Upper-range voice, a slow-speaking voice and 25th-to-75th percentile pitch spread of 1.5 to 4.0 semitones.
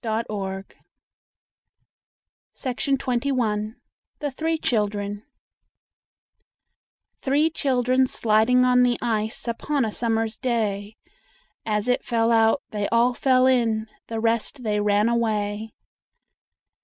Yes: high, 230 Hz; slow, 105 wpm; average, 2.9 semitones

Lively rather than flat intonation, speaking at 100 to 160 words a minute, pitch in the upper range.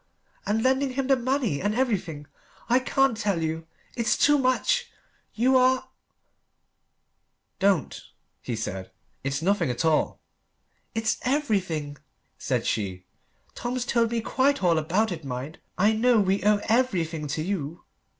Yes: wide, 8.0 semitones; average, 140 wpm; high, 210 Hz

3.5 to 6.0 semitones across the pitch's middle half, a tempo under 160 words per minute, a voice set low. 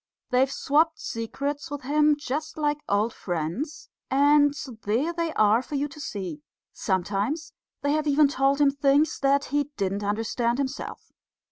No: average, 4.7 semitones; average, 150 wpm; very high, 275 Hz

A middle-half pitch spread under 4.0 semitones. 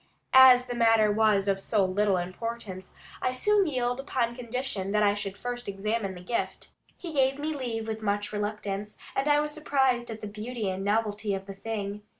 Yes: average, 3.6 semitones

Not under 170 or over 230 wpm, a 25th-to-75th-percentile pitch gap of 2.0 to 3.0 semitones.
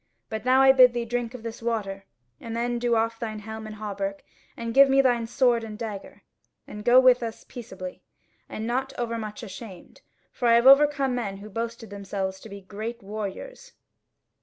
Yes: average, 190 wpm; average, 2.7 semitones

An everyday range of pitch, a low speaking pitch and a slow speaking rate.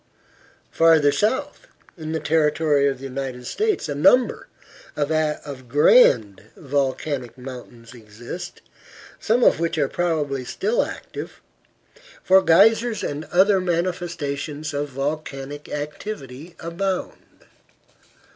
No: average, 4.3 semitones; medium, 150 Hz; slow, 105 wpm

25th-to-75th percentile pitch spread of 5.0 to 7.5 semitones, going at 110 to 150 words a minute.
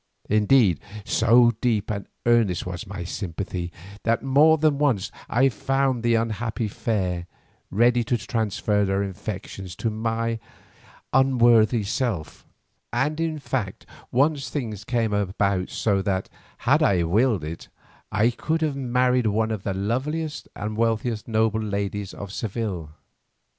No: average, 3.6 semitones; slow, 135 wpm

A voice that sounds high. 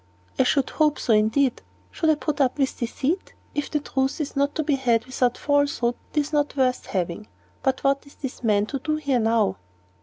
Yes: very high, 275 Hz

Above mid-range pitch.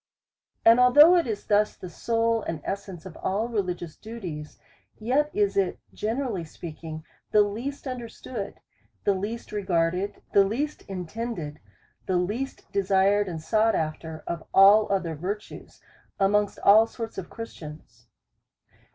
Yes: high, 200 Hz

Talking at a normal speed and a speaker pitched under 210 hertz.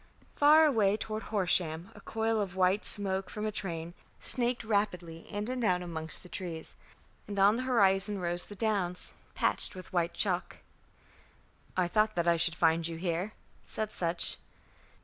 Yes: average, 165 wpm; high, 190 Hz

